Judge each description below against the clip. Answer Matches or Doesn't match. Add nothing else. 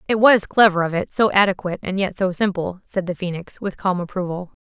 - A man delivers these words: Doesn't match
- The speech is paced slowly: Doesn't match